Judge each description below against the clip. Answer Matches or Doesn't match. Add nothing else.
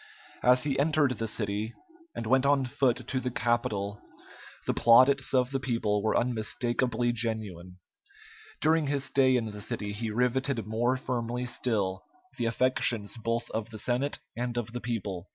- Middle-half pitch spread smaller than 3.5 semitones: Matches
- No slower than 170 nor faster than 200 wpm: Doesn't match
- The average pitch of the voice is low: Matches